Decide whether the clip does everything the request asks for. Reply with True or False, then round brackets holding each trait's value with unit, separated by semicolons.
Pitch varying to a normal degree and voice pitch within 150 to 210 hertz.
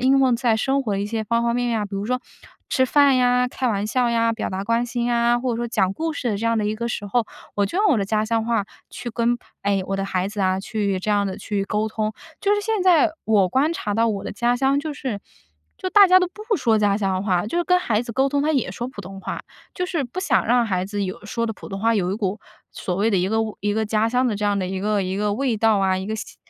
False (3.7 semitones; 225 Hz)